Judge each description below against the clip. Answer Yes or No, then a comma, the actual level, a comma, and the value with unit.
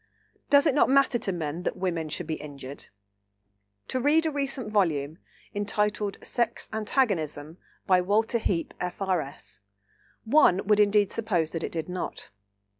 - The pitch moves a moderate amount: No, wide, 5.7 semitones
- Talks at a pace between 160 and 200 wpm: No, average, 145 wpm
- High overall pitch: Yes, high, 195 Hz